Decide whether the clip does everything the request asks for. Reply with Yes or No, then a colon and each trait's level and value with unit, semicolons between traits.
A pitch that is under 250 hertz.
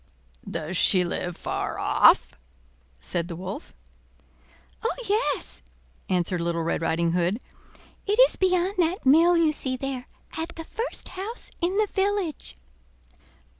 No: very high, 285 Hz